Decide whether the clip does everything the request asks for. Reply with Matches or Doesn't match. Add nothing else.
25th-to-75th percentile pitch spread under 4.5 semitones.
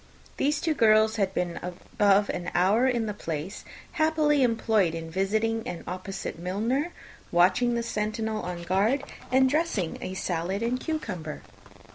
Doesn't match